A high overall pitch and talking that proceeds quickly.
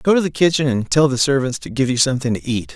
No: low, 135 Hz; fast, 305 wpm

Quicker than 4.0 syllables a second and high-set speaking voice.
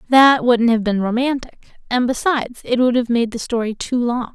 Yes: 5.0 syllables/s; high, 240 Hz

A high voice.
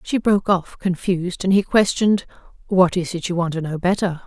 No: medium, 180 Hz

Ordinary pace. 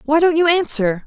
No: fast, 225 wpm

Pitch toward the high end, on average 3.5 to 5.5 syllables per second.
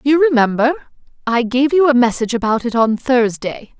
Yes: very high, 250 Hz; 5.1 syllables/s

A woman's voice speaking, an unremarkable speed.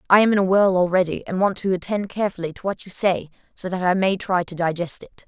No: female; fast, 260 wpm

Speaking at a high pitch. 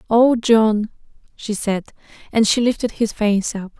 Yes: high, 220 Hz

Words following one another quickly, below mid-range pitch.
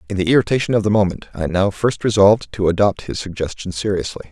Yes: fast, 210 wpm; low, 100 Hz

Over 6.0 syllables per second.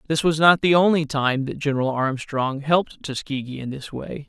No: 5.1 syllables/s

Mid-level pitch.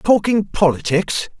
Yes: medium, 180 Hz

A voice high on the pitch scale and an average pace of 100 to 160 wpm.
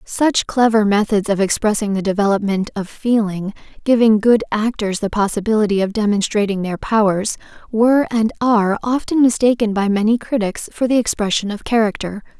Yes: high, 215 Hz; average, 150 wpm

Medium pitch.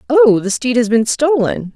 No: high, 230 Hz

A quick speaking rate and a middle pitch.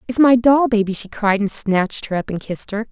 No: fast, 270 wpm; high, 220 Hz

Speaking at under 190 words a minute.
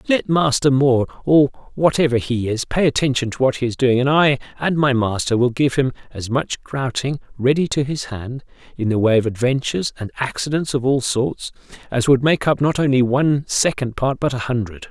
No: fast, 205 wpm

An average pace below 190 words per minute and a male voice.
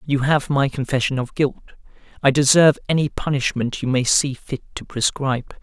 Yes: average, 170 wpm; male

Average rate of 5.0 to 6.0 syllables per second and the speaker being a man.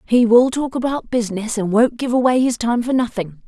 No: 5.4 syllables/s; female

